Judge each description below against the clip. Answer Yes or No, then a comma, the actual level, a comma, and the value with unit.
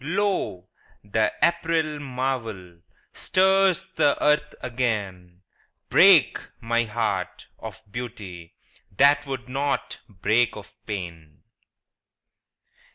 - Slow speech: Yes, slow, 90 wpm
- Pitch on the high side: No, low, 120 Hz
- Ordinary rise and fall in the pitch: No, wide, 6.6 semitones